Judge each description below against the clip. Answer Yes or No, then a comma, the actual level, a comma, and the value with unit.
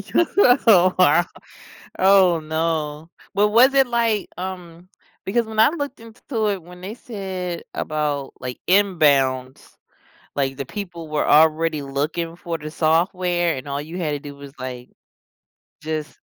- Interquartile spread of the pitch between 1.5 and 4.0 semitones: No, average, 4.8 semitones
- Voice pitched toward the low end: No, medium, 170 Hz